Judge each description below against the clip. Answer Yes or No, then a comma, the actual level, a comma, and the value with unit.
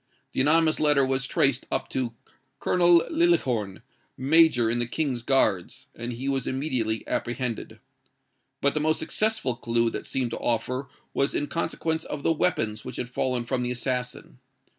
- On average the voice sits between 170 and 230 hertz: No, low, 130 Hz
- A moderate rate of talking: Yes, average, 160 wpm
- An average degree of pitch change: Yes, average, 4.2 semitones